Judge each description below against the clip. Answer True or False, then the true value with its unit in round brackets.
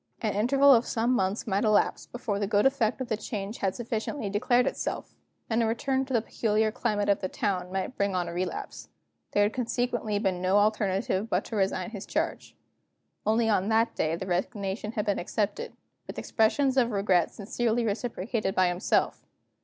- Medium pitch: False (215 Hz)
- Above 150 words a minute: True (185 wpm)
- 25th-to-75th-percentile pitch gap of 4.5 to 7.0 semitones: False (3.3 semitones)